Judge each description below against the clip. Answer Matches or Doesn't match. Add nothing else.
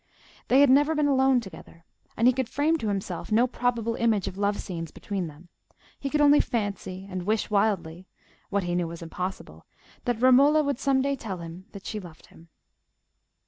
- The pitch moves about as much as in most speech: Doesn't match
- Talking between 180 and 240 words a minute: Matches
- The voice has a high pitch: Matches